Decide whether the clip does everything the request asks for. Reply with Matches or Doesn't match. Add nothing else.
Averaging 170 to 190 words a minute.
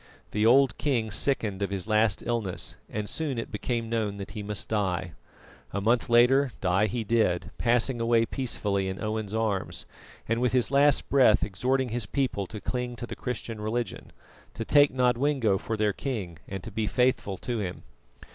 Matches